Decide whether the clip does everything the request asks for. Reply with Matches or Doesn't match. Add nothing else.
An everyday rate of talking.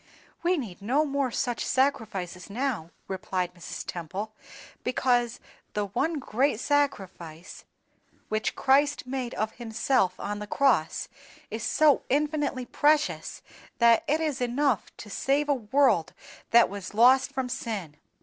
Doesn't match